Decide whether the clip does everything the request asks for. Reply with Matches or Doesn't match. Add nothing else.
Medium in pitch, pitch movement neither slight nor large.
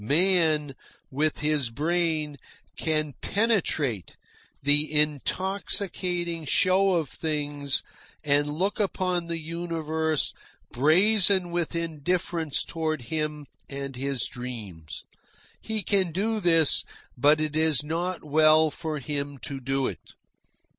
Matches